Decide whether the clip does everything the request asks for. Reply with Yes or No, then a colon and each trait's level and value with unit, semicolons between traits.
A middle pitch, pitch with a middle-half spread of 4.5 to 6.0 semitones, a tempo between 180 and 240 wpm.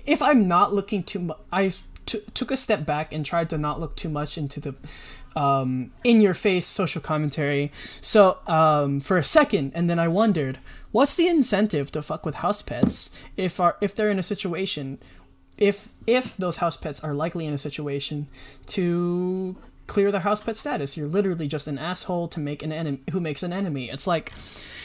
Yes: medium, 170 Hz; average, 5.3 semitones; average, 200 wpm